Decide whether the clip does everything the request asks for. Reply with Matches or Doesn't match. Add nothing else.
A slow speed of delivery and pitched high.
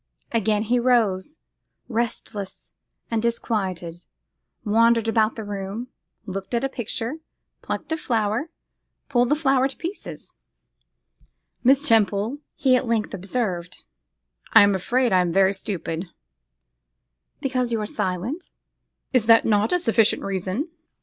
Matches